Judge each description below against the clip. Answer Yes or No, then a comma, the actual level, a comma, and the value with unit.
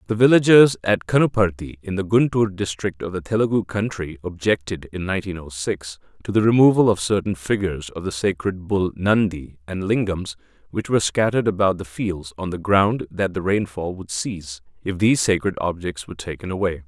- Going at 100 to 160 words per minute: No, average, 180 wpm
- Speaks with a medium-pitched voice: No, very low, 95 Hz